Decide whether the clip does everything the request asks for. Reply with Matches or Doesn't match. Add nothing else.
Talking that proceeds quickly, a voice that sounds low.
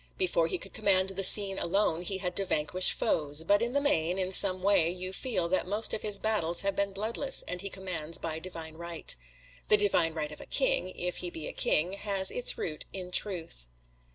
Doesn't match